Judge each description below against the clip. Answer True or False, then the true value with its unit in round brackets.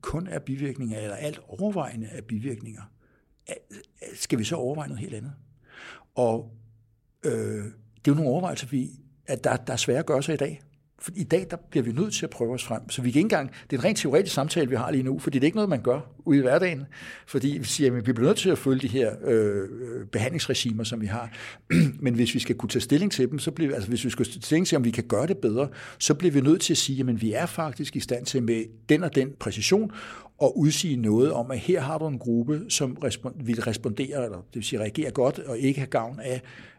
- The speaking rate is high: True (250 wpm)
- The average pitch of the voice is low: True (130 Hz)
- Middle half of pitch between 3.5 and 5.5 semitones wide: True (4.1 semitones)